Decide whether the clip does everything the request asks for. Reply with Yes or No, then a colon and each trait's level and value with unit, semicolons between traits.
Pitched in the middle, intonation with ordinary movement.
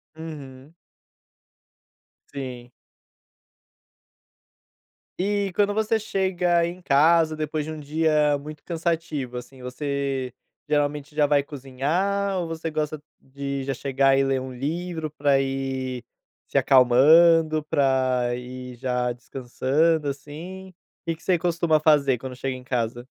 Yes: medium, 145 Hz; average, 3.7 semitones